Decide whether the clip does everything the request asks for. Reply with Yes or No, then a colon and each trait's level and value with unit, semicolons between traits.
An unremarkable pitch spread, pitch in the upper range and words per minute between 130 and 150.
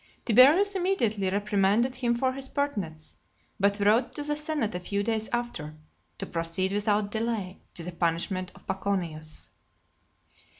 Yes: average, 4.9 semitones; high, 205 Hz; average, 140 wpm